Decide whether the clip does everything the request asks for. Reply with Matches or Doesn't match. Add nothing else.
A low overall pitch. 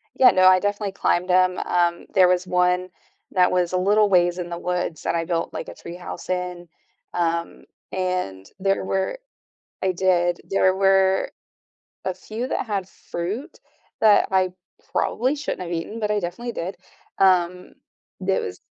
Doesn't match